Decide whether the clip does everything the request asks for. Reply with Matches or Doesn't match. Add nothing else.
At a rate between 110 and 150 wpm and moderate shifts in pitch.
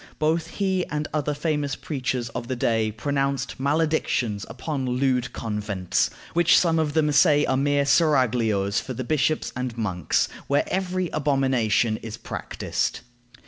Matches